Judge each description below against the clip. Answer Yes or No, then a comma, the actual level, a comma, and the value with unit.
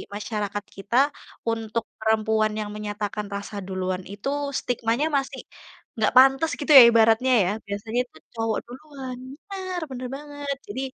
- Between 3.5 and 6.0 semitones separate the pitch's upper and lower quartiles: Yes, average, 4.1 semitones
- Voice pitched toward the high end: Yes, high, 225 Hz